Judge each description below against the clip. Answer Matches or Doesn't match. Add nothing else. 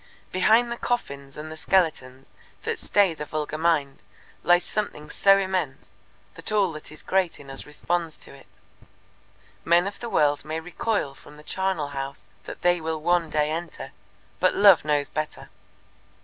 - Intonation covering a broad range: Doesn't match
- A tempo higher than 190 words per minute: Doesn't match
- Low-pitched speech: Doesn't match